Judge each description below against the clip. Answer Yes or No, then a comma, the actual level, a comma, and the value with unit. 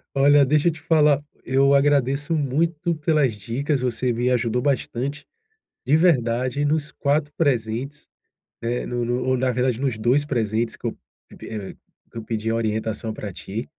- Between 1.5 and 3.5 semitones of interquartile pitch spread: No, average, 3.9 semitones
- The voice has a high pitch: No, low, 130 Hz